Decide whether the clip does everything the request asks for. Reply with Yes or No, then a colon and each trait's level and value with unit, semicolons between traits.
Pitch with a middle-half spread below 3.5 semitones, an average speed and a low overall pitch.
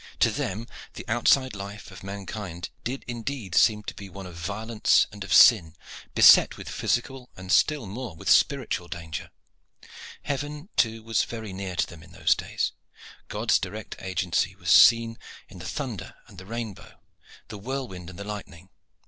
No: average, 4.0 semitones; average, 175 wpm; low, 105 Hz